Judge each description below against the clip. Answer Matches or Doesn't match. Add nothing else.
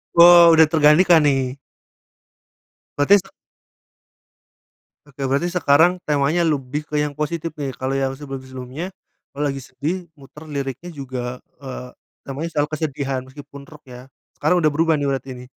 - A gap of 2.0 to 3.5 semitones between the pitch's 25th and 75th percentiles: Matches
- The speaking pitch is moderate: Matches